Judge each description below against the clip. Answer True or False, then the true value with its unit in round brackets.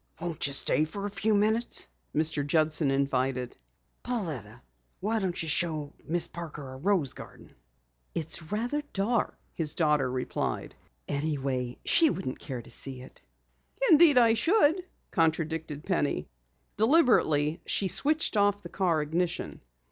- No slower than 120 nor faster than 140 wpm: True (135 wpm)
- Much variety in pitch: True (6.1 semitones)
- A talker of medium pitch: True (165 Hz)